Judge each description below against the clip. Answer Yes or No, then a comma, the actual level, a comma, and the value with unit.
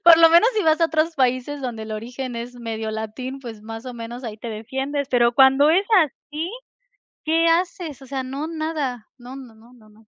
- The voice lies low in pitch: No, very high, 260 Hz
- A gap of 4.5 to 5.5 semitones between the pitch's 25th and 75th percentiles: Yes, average, 5.0 semitones